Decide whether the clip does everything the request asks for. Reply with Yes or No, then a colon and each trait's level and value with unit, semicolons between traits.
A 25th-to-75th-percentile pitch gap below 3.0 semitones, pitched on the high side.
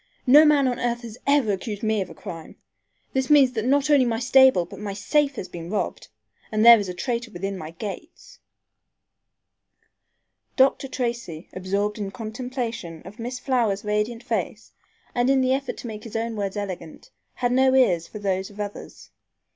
No: average, 4.3 semitones; high, 225 Hz